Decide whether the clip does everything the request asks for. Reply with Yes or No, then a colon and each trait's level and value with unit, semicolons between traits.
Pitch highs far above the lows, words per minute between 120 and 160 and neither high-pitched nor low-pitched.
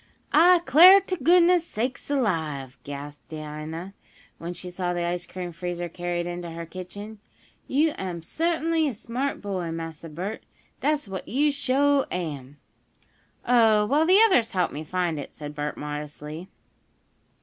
Yes: wide, 9.0 semitones; average, 150 wpm; medium, 180 Hz